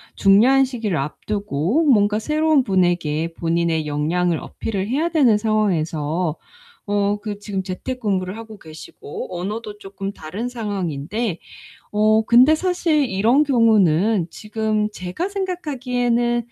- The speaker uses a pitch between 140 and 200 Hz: No, high, 210 Hz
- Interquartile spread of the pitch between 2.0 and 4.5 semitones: No, average, 5.2 semitones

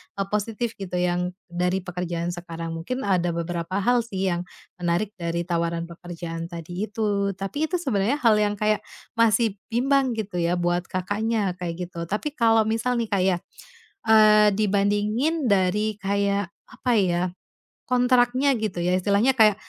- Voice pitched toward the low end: No, high, 200 Hz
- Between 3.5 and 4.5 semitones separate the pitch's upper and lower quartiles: Yes, average, 3.9 semitones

